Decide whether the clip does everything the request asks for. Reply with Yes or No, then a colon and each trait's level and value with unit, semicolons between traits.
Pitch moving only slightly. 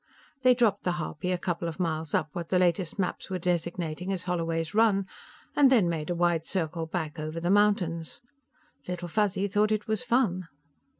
No: average, 3.4 semitones